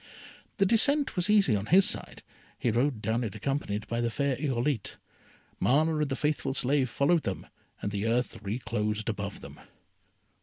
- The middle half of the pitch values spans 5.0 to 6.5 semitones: Yes, wide, 5.5 semitones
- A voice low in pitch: Yes, low, 125 Hz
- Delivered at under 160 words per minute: No, average, 165 wpm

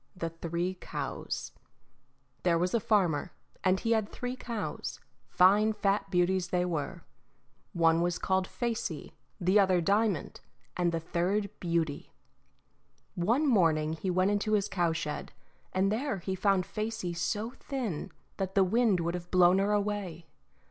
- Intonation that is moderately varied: Yes, average, 3.3 semitones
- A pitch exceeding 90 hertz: Yes, medium, 185 Hz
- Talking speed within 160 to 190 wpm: No, average, 145 wpm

